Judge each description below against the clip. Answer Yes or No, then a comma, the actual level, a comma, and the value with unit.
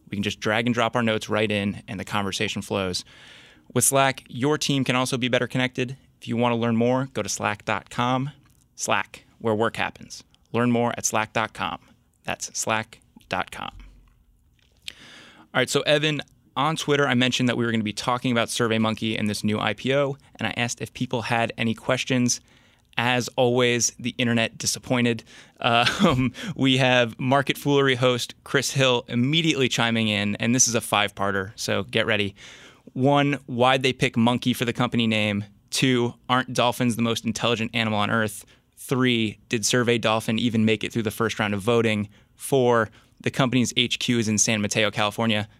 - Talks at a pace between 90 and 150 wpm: No, average, 180 wpm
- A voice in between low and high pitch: No, low, 120 Hz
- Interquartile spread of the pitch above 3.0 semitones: No, narrow, 2.5 semitones